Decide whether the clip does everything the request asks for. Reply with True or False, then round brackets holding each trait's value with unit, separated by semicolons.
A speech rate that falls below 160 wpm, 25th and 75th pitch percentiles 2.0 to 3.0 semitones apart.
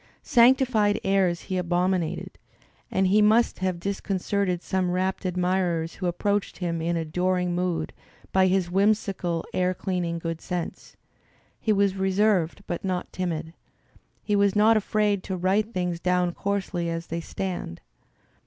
True (150 wpm; 2.5 semitones)